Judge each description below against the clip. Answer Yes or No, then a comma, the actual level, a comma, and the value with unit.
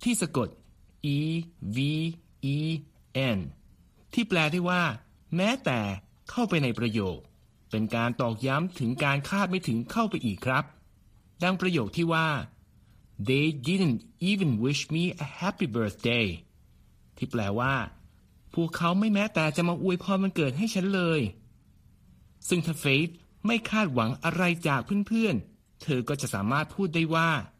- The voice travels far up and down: Yes, wide, 7.1 semitones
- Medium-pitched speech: Yes, medium, 155 Hz